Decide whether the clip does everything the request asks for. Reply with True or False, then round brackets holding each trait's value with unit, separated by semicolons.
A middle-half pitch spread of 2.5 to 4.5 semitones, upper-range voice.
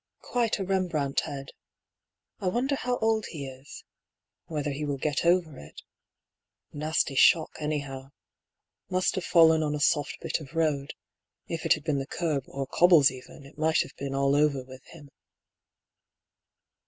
False (3.6 semitones; 150 Hz)